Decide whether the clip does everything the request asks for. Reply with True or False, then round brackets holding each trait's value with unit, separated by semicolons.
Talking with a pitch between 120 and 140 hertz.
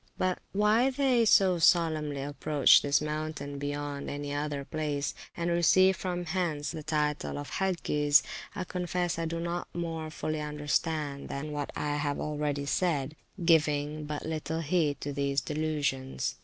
False (150 Hz)